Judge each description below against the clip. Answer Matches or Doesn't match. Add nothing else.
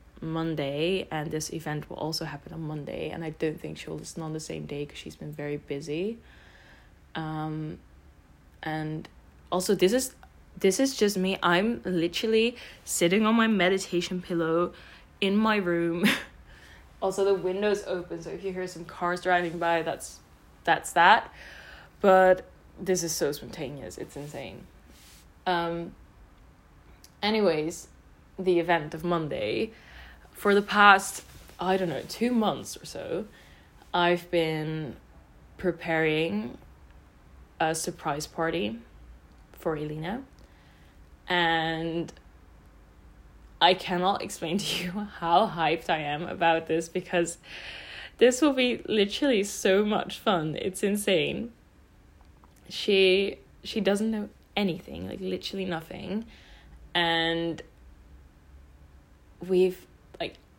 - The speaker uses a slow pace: Matches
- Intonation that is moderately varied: Matches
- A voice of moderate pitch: Matches